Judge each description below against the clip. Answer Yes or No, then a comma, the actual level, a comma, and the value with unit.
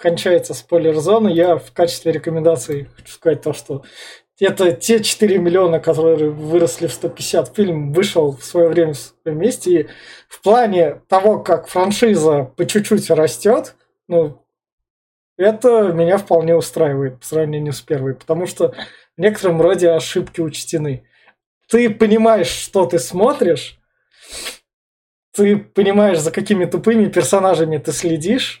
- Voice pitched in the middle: Yes, medium, 170 Hz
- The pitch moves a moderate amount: Yes, average, 3.7 semitones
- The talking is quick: No, average, 130 wpm